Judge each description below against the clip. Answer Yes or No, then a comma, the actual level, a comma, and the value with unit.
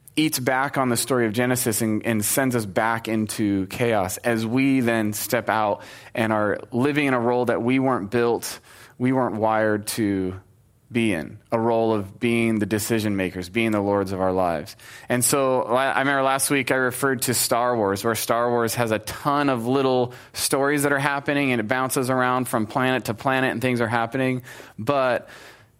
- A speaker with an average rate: Yes, average, 195 wpm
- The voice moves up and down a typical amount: Yes, average, 3.1 semitones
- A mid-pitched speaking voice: No, low, 120 Hz